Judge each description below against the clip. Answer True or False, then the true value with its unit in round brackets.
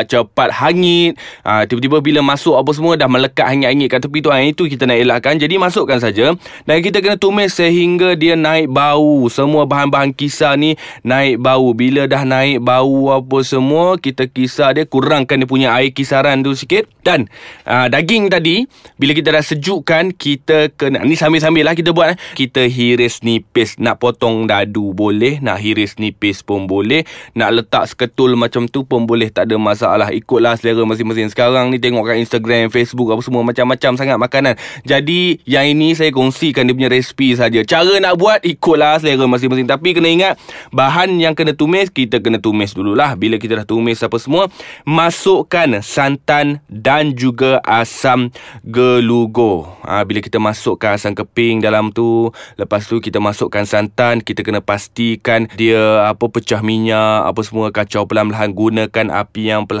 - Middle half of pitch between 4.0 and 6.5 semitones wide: True (4.9 semitones)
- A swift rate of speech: True (170 wpm)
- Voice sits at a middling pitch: False (130 Hz)